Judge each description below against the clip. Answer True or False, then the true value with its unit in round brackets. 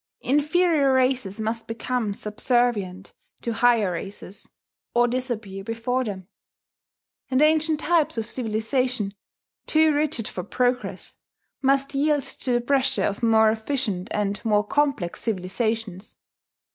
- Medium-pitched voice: False (240 Hz)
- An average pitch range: True (4.3 semitones)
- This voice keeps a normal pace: False (120 wpm)